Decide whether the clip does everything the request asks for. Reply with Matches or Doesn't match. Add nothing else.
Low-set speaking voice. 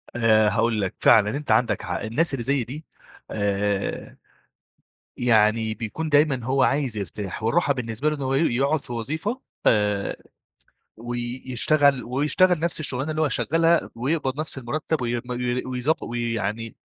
Matches